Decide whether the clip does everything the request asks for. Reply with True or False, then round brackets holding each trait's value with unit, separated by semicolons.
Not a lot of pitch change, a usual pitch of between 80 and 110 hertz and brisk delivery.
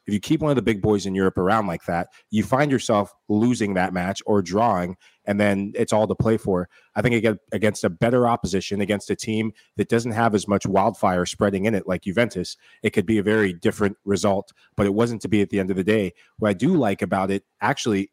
True (2.3 semitones; 105 Hz; 240 wpm)